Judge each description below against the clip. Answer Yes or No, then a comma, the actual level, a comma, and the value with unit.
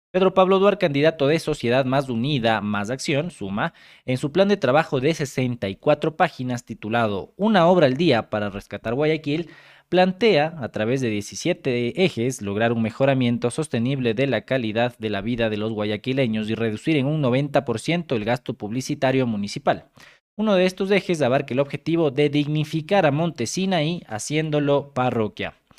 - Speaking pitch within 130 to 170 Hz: Yes, low, 135 Hz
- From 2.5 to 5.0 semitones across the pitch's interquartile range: No, wide, 5.4 semitones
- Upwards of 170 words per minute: No, average, 160 wpm